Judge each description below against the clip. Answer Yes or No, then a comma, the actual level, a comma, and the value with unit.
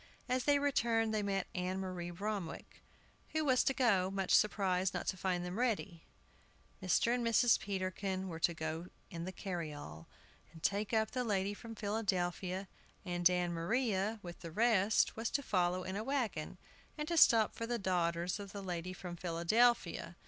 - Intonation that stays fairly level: No, average, 4.2 semitones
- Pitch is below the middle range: No, high, 190 Hz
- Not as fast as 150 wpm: No, average, 175 wpm